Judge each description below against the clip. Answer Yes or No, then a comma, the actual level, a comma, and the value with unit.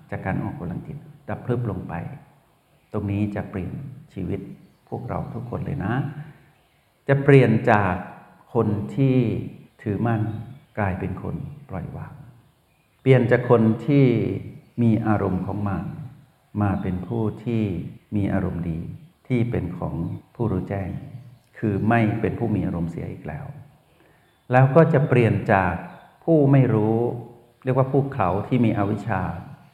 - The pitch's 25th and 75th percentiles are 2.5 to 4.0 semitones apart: No, average, 5.0 semitones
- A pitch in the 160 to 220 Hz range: No, low, 115 Hz